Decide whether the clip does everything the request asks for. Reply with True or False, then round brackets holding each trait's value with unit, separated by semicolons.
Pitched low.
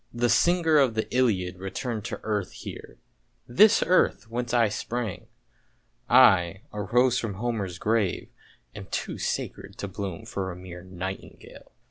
True (110 Hz)